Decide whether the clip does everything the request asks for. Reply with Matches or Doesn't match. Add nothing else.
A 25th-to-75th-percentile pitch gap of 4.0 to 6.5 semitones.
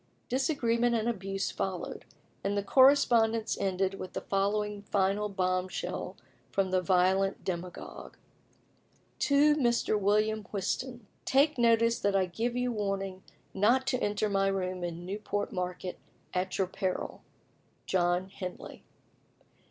Doesn't match